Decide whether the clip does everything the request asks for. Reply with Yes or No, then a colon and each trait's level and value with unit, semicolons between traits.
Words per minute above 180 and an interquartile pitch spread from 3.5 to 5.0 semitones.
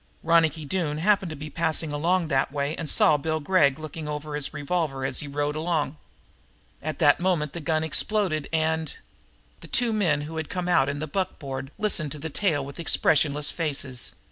No: average, 190 wpm; narrow, 2.4 semitones